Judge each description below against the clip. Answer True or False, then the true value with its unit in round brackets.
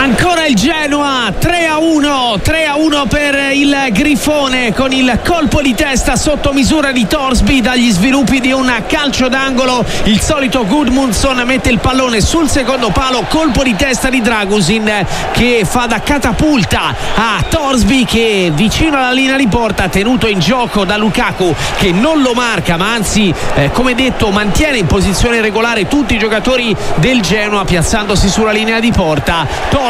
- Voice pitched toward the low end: False (250 Hz)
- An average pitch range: True (4.2 semitones)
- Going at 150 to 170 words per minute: True (165 wpm)